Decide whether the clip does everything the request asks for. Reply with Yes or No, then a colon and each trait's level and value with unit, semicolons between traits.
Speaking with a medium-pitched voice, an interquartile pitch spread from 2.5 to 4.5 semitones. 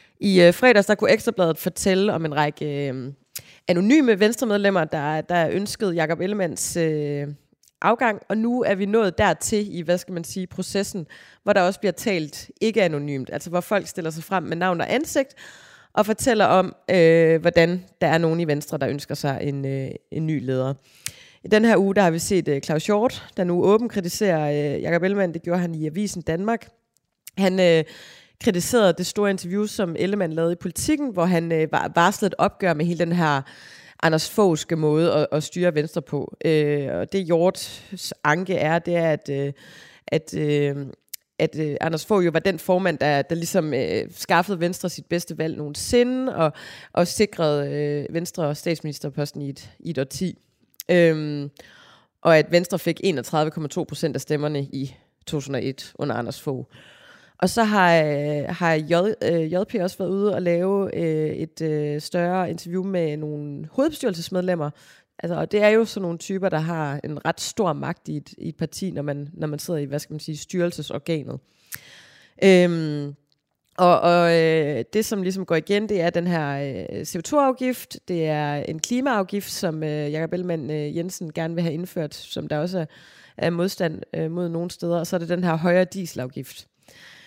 Yes: medium, 170 Hz; average, 3.9 semitones